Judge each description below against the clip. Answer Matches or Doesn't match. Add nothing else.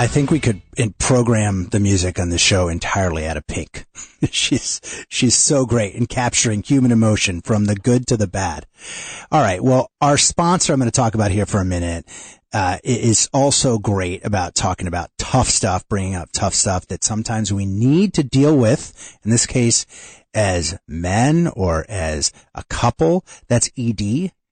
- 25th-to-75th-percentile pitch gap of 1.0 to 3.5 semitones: Doesn't match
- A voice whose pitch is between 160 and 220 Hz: Doesn't match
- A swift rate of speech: Doesn't match